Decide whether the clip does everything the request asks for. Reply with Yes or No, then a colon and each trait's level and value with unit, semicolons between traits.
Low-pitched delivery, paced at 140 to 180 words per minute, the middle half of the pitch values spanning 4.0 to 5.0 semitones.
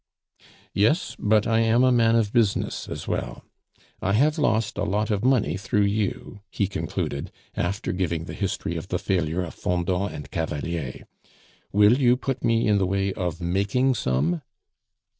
Yes: low, 100 Hz; average, 165 wpm; average, 4.4 semitones